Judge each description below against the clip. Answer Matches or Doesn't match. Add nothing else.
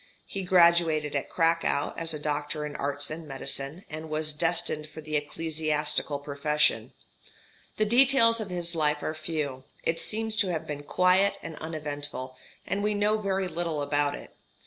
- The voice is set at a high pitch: Doesn't match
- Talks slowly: Doesn't match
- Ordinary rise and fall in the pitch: Matches